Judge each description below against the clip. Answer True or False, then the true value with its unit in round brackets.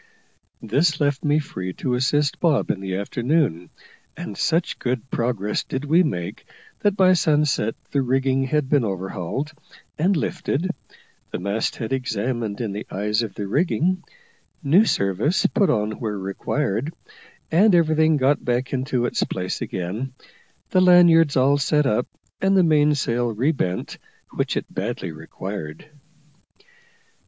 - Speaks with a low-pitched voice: True (130 Hz)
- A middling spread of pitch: False (6.6 semitones)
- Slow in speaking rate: False (145 wpm)